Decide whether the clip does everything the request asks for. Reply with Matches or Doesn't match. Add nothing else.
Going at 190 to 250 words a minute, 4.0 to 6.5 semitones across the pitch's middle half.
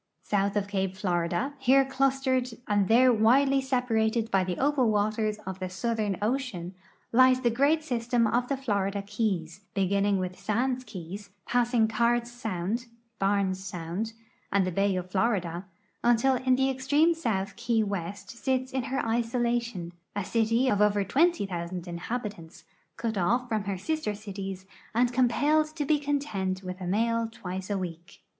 Doesn't match